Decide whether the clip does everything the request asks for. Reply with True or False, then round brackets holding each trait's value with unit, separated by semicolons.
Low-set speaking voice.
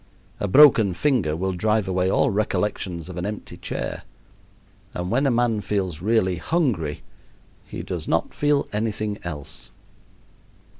True (100 Hz)